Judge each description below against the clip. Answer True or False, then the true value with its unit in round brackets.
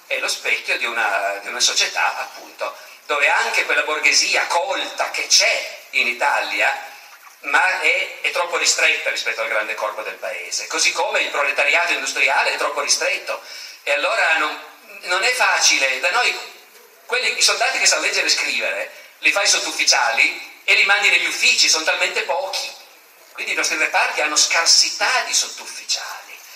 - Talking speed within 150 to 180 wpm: True (165 wpm)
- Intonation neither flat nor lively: False (8.5 semitones)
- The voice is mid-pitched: True (175 Hz)